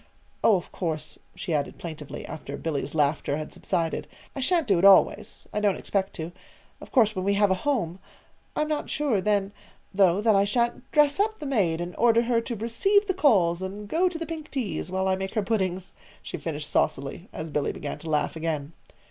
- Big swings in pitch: Yes, wide, 6.3 semitones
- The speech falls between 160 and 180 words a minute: No, fast, 205 wpm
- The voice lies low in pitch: No, high, 195 Hz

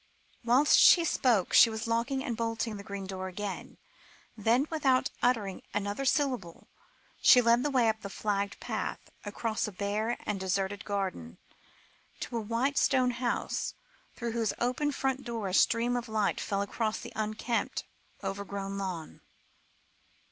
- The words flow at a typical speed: Yes, average, 150 wpm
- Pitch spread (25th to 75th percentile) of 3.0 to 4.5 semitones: Yes, average, 3.4 semitones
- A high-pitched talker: Yes, high, 220 Hz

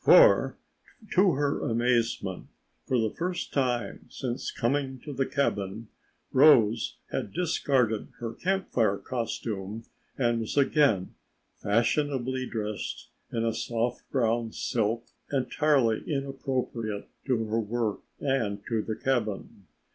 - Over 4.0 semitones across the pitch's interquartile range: No, average, 3.5 semitones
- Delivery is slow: Yes, slow, 115 wpm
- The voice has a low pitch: Yes, low, 120 Hz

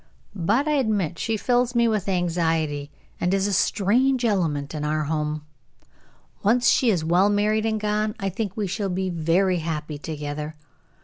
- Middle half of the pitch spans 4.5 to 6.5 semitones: Yes, average, 5.2 semitones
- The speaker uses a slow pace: No, average, 170 wpm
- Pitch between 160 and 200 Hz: Yes, high, 190 Hz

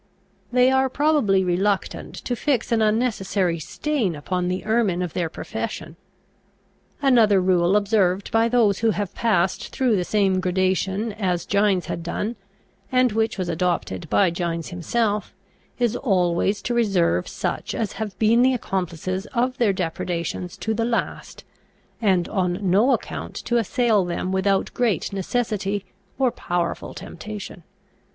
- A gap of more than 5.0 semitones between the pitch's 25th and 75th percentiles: No, average, 4.2 semitones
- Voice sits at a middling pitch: No, high, 200 Hz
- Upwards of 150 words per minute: No, average, 145 wpm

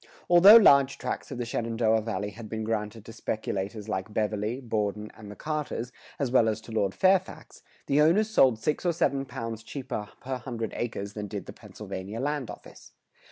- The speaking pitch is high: No, low, 115 Hz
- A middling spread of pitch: Yes, average, 4.4 semitones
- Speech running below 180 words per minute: No, average, 185 wpm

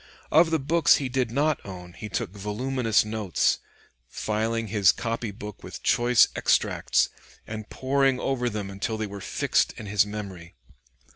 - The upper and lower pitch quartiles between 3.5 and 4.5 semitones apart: Yes, average, 3.8 semitones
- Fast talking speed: No, average, 155 wpm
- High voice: No, low, 110 Hz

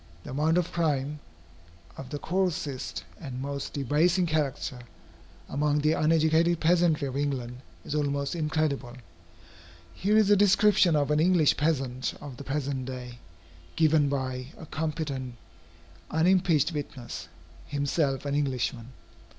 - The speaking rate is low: Yes, slow, 125 wpm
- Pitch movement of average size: Yes, average, 3.1 semitones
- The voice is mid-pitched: Yes, medium, 145 Hz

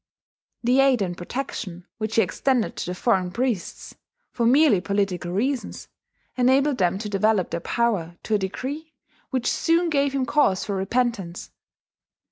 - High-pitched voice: Yes, high, 225 Hz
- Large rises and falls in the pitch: Yes, wide, 5.7 semitones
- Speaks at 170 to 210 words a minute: No, average, 150 wpm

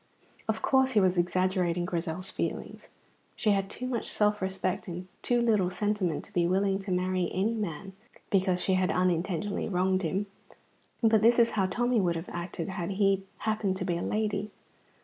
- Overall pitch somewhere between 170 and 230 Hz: Yes, high, 190 Hz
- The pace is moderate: Yes, average, 180 wpm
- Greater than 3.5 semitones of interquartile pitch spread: No, narrow, 2.6 semitones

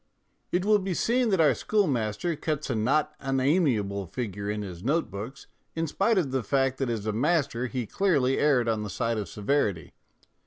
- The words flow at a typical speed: Yes, average, 190 wpm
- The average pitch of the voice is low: Yes, low, 130 Hz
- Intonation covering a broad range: Yes, wide, 7.0 semitones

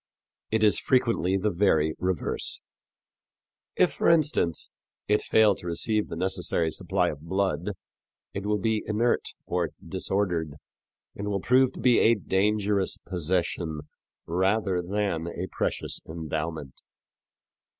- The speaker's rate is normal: No, slow, 125 wpm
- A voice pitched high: No, very low, 95 Hz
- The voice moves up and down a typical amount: Yes, average, 3.8 semitones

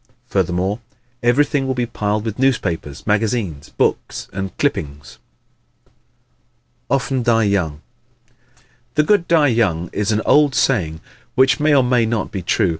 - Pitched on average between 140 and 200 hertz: No, low, 110 Hz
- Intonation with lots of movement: Yes, wide, 5.8 semitones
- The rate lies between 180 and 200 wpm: No, average, 140 wpm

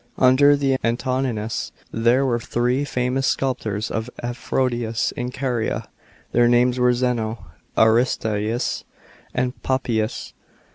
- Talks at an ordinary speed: No, slow, 105 wpm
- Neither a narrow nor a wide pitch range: No, narrow, 2.0 semitones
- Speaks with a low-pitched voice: Yes, low, 125 Hz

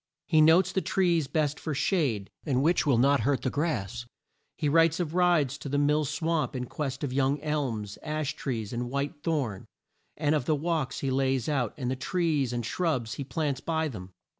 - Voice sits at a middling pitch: Yes, medium, 145 Hz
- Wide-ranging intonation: No, average, 3.6 semitones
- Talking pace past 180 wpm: Yes, average, 200 wpm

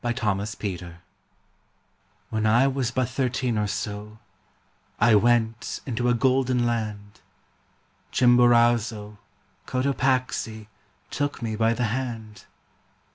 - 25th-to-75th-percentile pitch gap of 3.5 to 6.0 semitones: No, average, 2.8 semitones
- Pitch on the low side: Yes, low, 115 Hz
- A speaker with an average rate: No, slow, 105 wpm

